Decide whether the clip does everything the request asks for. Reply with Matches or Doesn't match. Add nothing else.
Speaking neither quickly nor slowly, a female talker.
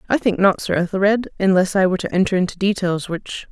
Doesn't match